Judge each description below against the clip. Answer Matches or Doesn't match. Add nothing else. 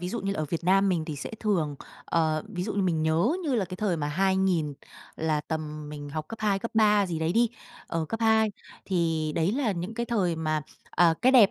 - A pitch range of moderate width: Matches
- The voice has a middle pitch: Matches